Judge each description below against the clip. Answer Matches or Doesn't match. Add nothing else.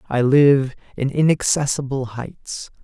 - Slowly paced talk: Matches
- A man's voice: Matches